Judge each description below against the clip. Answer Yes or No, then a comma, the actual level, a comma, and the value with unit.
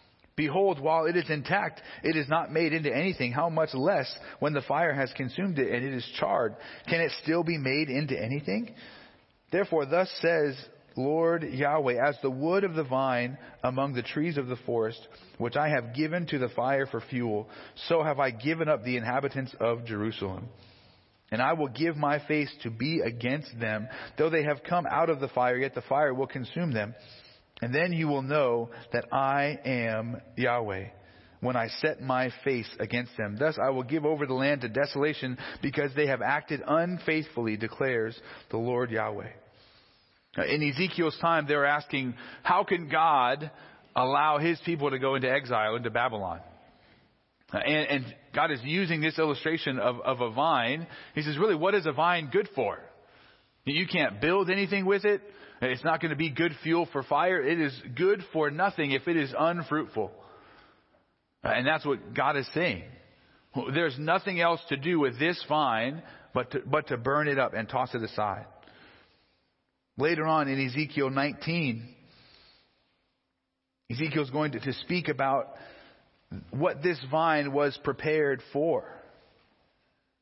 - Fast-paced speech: No, average, 170 wpm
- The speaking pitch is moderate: Yes, medium, 145 Hz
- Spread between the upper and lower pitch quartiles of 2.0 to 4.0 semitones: No, average, 4.4 semitones